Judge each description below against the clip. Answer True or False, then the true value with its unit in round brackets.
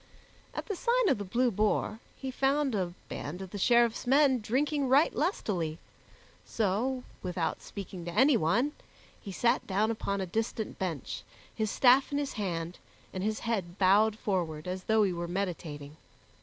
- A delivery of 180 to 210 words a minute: False (165 wpm)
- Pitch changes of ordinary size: False (5.7 semitones)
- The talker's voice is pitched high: True (210 Hz)